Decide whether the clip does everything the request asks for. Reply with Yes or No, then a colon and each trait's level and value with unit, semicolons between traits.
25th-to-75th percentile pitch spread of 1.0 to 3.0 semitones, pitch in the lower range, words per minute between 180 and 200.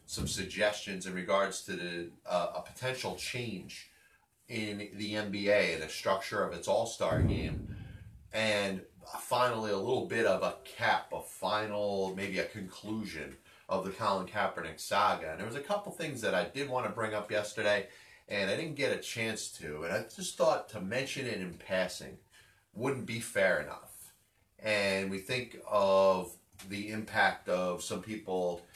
No: narrow, 2.5 semitones; low, 105 Hz; average, 170 wpm